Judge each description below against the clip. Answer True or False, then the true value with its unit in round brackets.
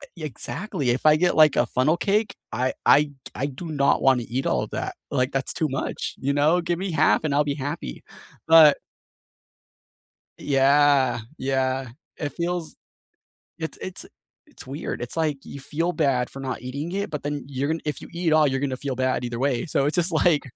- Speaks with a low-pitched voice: False (145 Hz)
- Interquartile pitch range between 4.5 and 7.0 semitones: False (3.3 semitones)